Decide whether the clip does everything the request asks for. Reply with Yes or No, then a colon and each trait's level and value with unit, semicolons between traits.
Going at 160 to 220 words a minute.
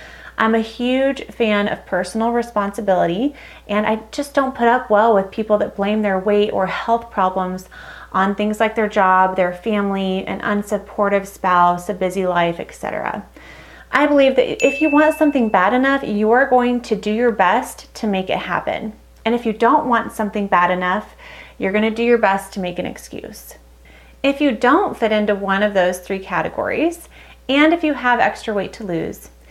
Yes: average, 190 wpm